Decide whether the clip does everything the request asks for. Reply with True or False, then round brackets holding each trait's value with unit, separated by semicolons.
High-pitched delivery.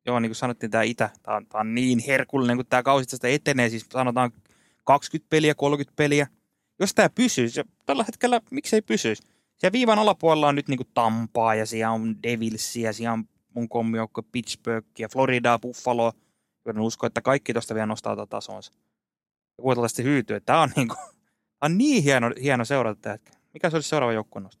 False (120 Hz)